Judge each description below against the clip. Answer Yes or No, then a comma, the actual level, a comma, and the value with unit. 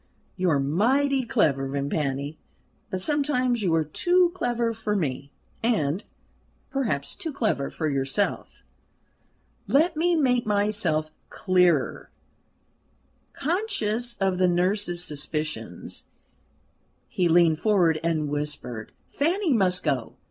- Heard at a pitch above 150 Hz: Yes, medium, 185 Hz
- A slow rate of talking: Yes, slow, 110 wpm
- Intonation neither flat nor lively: No, wide, 8.1 semitones